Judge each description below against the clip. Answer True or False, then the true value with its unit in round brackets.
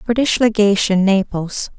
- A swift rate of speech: False (100 wpm)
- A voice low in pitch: False (205 Hz)